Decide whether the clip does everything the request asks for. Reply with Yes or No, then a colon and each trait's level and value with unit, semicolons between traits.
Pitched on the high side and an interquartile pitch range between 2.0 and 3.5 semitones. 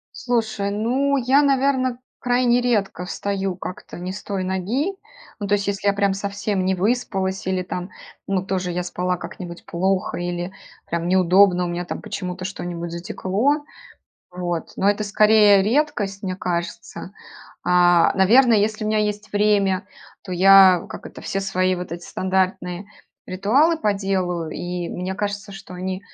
Yes: high, 195 Hz; average, 2.7 semitones